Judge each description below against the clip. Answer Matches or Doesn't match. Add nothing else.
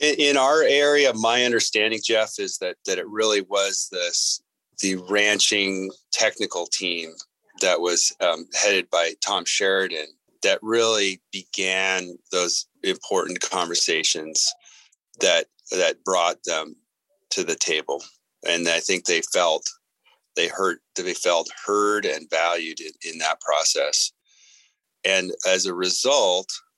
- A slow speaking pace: Matches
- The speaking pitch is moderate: Doesn't match